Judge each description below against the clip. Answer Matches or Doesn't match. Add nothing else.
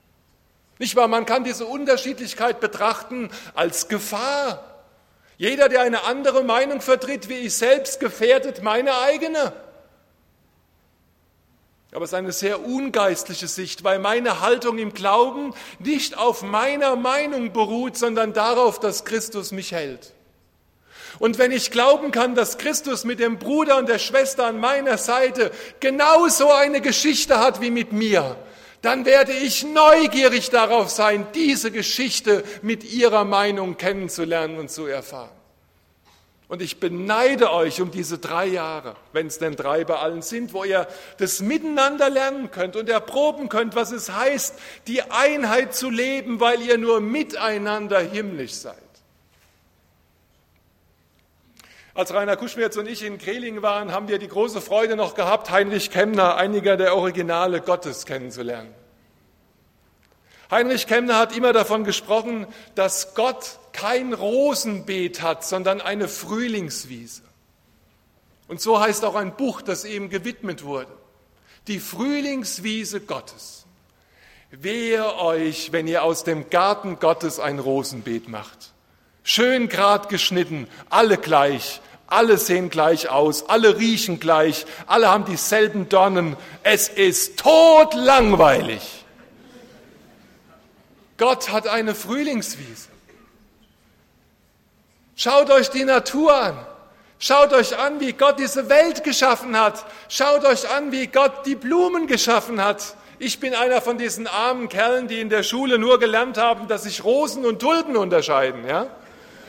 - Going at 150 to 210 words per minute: Doesn't match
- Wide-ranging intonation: Matches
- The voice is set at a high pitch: Matches